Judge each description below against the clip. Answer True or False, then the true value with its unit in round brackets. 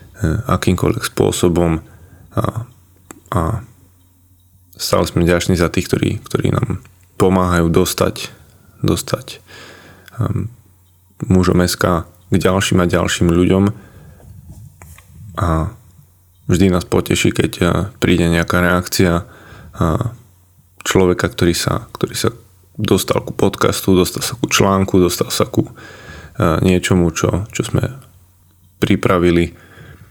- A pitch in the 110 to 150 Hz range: False (90 Hz)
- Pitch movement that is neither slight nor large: False (2.2 semitones)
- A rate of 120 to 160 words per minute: False (110 wpm)